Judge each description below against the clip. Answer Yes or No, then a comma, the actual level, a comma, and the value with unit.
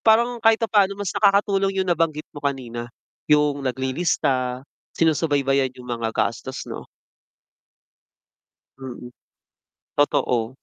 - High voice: No, medium, 145 Hz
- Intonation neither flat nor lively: No, wide, 6.9 semitones